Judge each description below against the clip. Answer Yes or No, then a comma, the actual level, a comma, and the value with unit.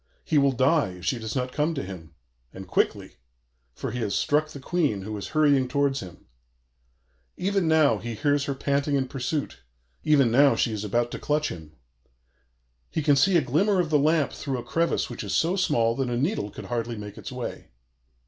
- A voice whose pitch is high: No, low, 135 Hz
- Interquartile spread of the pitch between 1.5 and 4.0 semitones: No, average, 5.0 semitones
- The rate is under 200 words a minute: No, fast, 205 wpm